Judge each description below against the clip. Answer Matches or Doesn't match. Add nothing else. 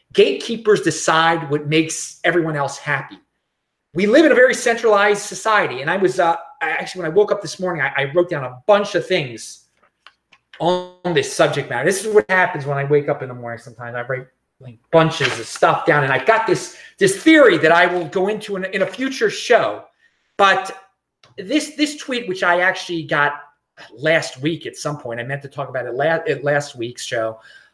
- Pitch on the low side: Doesn't match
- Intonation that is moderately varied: Doesn't match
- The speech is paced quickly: Matches